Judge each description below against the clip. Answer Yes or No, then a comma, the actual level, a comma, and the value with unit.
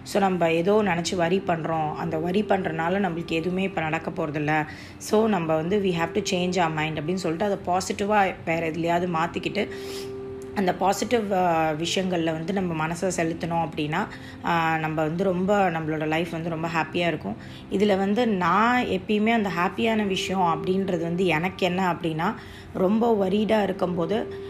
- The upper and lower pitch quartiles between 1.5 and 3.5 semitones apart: Yes, average, 3.2 semitones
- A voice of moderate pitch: Yes, medium, 180 Hz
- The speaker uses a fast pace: Yes, fast, 155 wpm